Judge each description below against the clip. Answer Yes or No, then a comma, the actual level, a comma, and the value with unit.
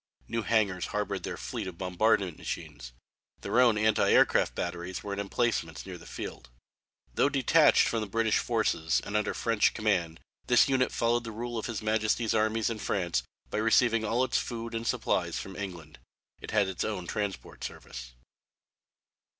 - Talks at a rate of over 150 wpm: Yes, average, 175 wpm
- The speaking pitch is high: No, low, 110 Hz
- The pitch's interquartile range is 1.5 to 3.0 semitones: No, average, 3.7 semitones